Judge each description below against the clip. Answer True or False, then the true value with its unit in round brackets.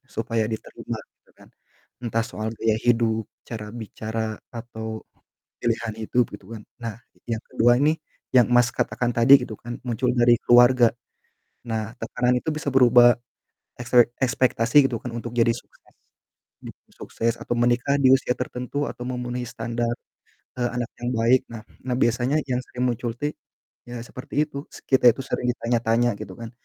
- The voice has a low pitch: True (120 Hz)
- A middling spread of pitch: False (1.4 semitones)